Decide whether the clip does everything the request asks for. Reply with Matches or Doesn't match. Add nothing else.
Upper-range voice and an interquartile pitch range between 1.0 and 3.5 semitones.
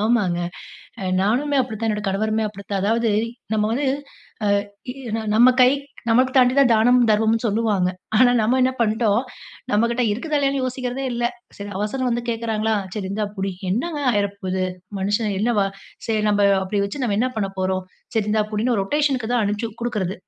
Matches